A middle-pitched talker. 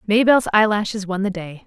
No: high, 205 Hz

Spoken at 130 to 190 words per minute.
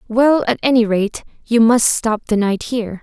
No: average, 200 wpm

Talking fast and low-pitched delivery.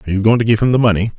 Yes: fast, 405 wpm; low, 110 Hz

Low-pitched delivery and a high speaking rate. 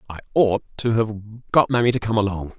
Yes: low, 110 Hz; fast, 210 wpm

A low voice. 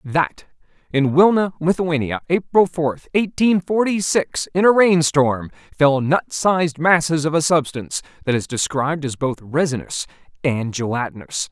No: medium, 155 Hz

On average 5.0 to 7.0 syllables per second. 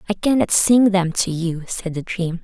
No: 4.6 syllables/s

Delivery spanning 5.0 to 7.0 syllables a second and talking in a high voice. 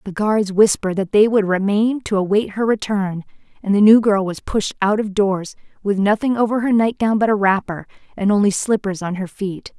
Yes: 5.2 syllables/s; high, 205 Hz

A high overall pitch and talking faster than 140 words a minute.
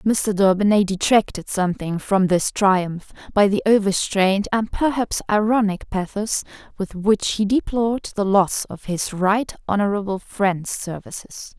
No: high, 200 Hz; slow, 135 wpm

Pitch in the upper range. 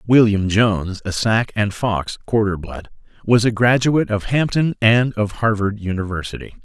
No: low, 110 Hz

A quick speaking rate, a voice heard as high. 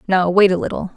No: fast, 250 wpm; medium, 180 Hz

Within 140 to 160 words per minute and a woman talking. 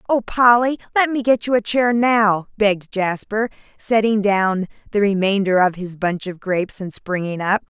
No: average, 175 wpm; female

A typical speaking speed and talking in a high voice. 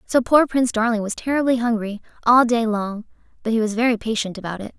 No: fast, 215 wpm; high, 230 Hz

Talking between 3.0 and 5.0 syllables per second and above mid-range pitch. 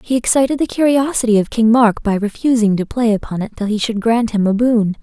No: 5.7 syllables/s; high, 225 Hz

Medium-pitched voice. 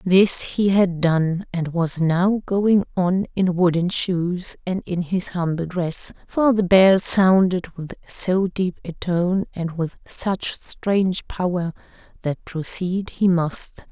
Yes: medium, 180 Hz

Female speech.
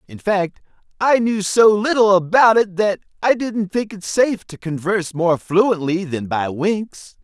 No: male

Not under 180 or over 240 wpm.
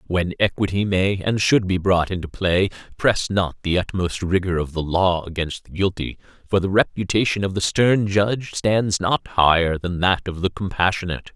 Yes: average, 185 wpm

